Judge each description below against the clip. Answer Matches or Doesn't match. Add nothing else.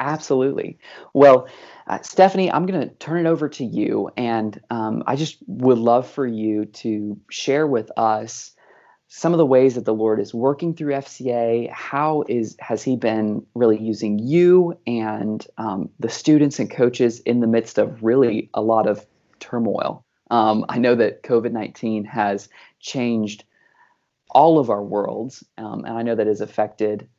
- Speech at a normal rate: Matches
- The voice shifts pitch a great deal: Doesn't match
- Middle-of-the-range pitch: Doesn't match